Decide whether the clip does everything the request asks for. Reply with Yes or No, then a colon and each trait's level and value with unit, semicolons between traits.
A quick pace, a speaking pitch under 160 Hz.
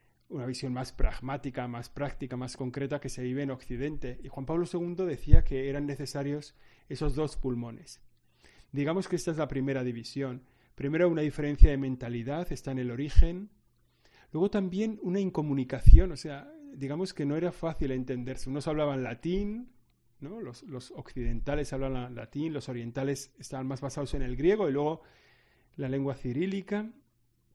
No: average, 165 wpm; medium, 140 Hz